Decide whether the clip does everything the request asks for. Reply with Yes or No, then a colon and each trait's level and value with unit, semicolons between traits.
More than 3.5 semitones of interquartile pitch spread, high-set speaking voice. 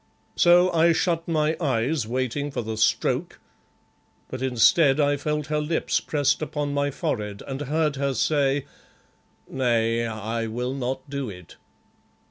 No: average, 4.2 semitones; medium, 140 Hz